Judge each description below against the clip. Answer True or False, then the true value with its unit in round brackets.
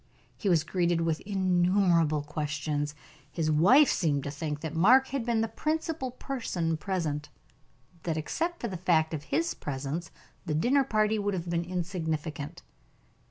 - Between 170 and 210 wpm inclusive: False (155 wpm)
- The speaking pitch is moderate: True (170 Hz)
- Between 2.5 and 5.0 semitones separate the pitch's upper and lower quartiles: False (5.5 semitones)